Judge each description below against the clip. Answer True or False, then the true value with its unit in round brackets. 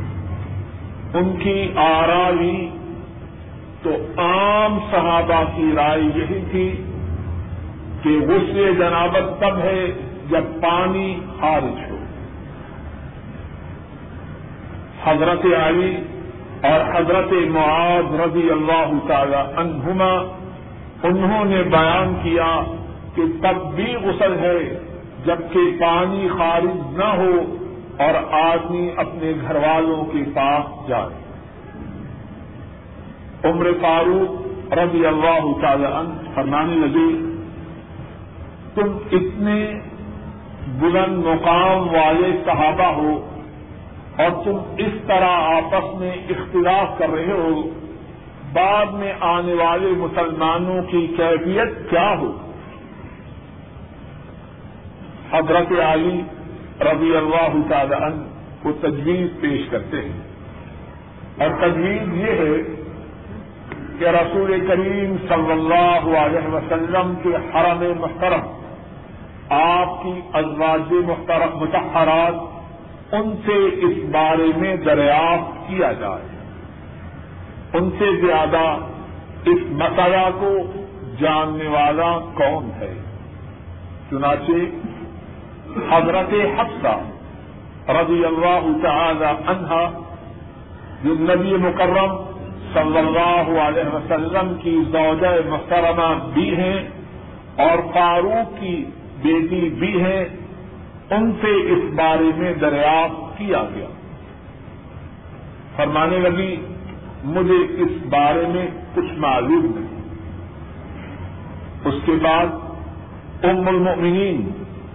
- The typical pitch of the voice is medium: True (170 Hz)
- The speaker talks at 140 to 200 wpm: False (95 wpm)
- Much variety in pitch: False (2.9 semitones)